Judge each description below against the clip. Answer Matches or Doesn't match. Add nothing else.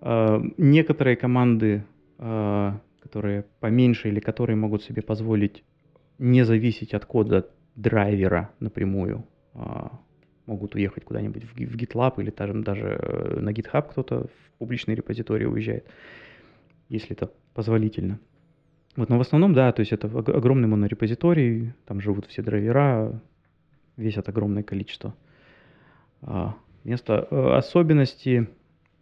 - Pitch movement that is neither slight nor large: Matches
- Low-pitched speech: Matches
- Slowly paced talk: Matches